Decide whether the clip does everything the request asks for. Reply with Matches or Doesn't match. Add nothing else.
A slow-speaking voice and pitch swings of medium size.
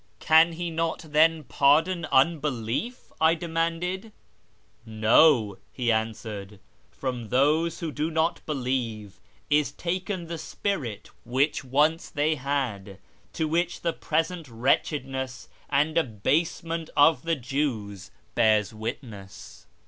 Doesn't match